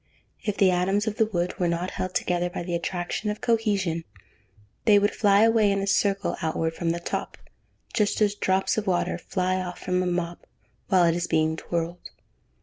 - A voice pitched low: No, medium, 185 Hz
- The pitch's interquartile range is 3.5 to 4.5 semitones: No, average, 2.8 semitones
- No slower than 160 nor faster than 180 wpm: No, average, 195 wpm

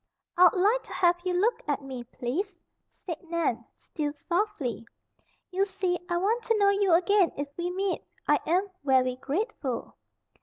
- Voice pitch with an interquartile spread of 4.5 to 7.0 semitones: Yes, wide, 5.6 semitones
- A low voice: No, very high, 350 Hz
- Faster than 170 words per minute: No, average, 160 wpm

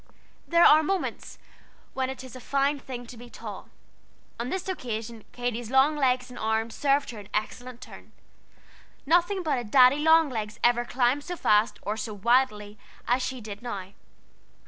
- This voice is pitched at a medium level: No, very high, 250 Hz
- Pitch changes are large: No, average, 3.9 semitones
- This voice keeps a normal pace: Yes, average, 170 wpm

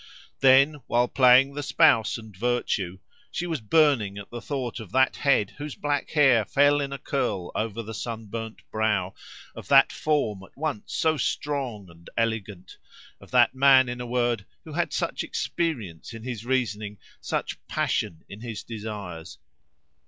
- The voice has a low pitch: Yes, low, 120 Hz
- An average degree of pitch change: Yes, average, 4.6 semitones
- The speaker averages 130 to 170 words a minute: Yes, average, 160 wpm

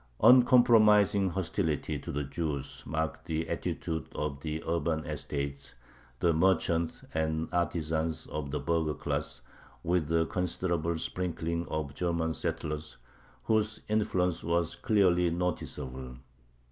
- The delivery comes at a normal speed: No, slow, 115 wpm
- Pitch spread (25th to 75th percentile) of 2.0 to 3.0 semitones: Yes, narrow, 2.4 semitones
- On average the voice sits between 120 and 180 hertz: No, very low, 80 Hz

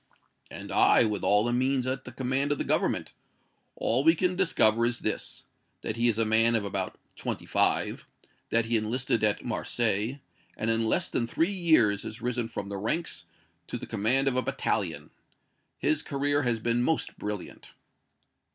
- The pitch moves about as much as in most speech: Yes, average, 3.6 semitones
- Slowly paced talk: No, average, 180 wpm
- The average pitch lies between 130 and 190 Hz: No, low, 120 Hz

